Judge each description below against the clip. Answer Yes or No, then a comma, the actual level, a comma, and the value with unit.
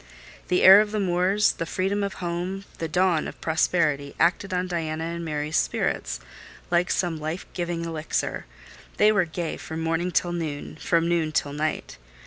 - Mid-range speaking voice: Yes, medium, 170 Hz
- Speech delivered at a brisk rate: No, average, 175 wpm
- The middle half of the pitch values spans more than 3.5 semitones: No, narrow, 2.4 semitones